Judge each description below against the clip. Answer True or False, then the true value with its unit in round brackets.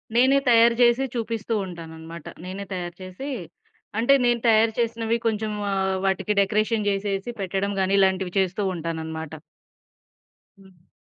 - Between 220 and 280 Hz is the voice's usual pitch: False (195 Hz)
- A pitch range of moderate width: True (3.8 semitones)